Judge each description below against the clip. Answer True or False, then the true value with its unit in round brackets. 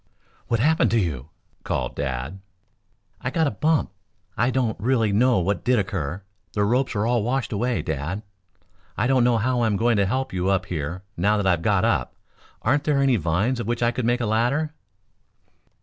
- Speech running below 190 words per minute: False (195 wpm)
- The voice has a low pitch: True (115 Hz)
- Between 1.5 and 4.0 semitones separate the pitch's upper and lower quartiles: False (4.7 semitones)